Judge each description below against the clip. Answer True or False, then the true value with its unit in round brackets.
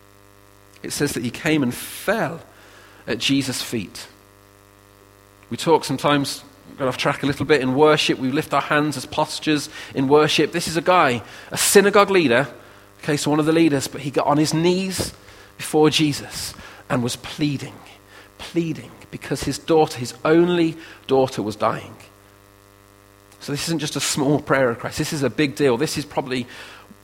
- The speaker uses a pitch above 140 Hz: False (135 Hz)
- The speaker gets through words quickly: False (175 wpm)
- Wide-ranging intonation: True (7.3 semitones)